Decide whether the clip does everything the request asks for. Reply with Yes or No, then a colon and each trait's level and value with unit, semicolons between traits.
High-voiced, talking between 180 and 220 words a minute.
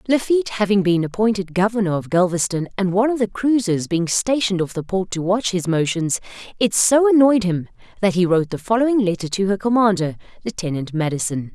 Yes: high, 195 Hz; average, 185 wpm